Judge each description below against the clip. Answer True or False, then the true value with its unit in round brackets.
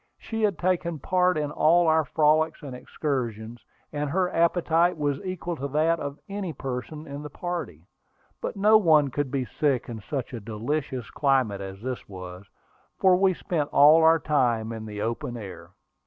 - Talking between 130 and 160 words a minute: False (175 wpm)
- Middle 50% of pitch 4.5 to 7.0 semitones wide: True (5.5 semitones)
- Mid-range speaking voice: True (145 Hz)